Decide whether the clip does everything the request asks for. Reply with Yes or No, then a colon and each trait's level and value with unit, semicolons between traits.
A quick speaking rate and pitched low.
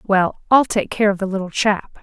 No: fast, 240 wpm; high, 200 Hz